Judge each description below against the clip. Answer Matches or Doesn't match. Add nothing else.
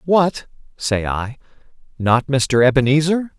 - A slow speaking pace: Matches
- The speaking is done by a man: Matches